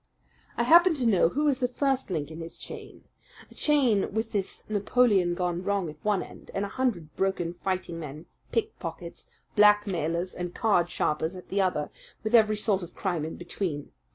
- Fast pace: No, average, 180 wpm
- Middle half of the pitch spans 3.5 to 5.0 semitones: Yes, average, 4.3 semitones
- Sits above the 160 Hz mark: Yes, high, 190 Hz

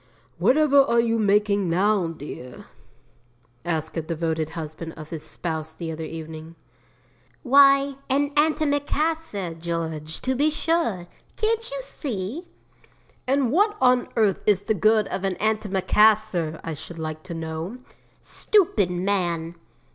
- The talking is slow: Yes, slow, 130 wpm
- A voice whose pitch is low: No, high, 200 Hz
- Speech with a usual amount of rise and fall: No, wide, 8.8 semitones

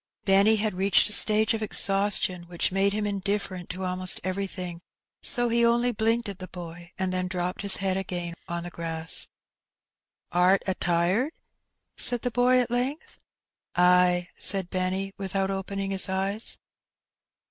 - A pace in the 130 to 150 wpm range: No, average, 160 wpm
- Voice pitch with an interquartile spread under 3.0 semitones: Yes, narrow, 2.6 semitones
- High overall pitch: Yes, high, 195 Hz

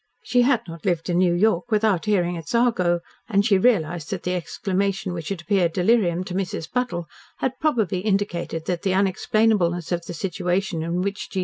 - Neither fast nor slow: Yes, average, 190 wpm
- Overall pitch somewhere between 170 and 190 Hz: Yes, medium, 185 Hz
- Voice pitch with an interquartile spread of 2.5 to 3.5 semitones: Yes, average, 3.2 semitones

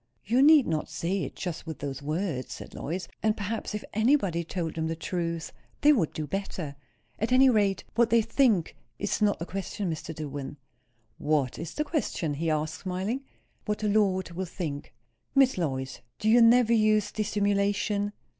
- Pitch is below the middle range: No, high, 190 Hz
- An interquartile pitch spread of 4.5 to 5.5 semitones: Yes, average, 5.2 semitones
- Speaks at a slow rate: No, average, 175 wpm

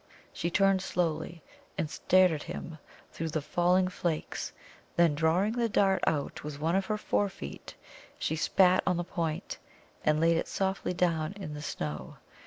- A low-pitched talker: No, medium, 170 Hz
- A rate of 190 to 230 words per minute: No, average, 165 wpm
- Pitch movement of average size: Yes, average, 3.2 semitones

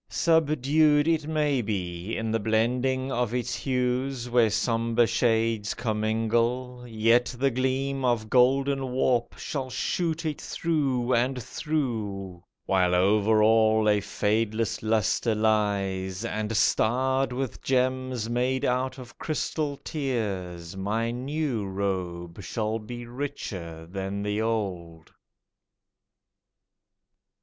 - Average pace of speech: No, slow, 110 wpm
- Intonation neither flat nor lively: Yes, average, 3.6 semitones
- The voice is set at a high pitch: No, low, 115 Hz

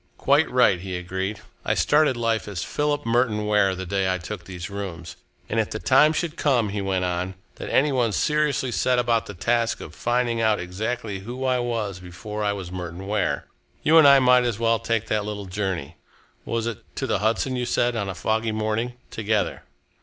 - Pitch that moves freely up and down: No, average, 4.1 semitones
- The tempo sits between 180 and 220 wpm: Yes, fast, 205 wpm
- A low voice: Yes, low, 110 Hz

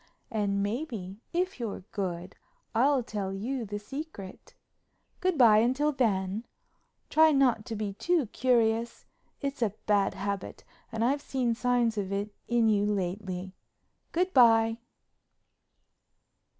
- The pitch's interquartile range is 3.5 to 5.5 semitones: Yes, average, 4.3 semitones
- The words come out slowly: Yes, slow, 125 wpm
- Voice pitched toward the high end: Yes, high, 225 Hz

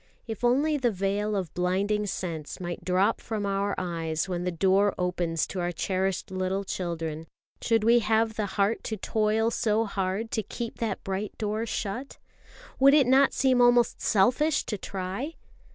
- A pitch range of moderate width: Yes, average, 3.6 semitones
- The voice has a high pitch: Yes, high, 205 Hz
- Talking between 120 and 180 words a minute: Yes, average, 170 wpm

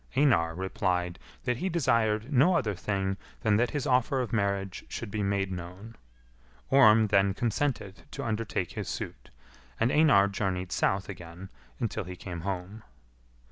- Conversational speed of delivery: Yes, average, 150 wpm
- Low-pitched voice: Yes, low, 100 Hz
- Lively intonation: No, average, 3.8 semitones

